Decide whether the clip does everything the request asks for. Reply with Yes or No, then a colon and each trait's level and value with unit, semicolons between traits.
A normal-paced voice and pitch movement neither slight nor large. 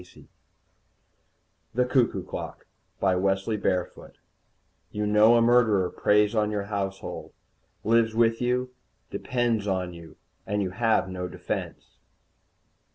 No: slow, 120 wpm; average, 3.1 semitones